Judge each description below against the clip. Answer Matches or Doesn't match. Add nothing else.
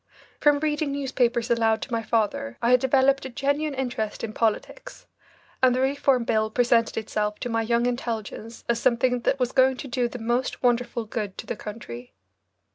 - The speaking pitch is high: Matches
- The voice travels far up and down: Doesn't match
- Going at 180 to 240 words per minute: Matches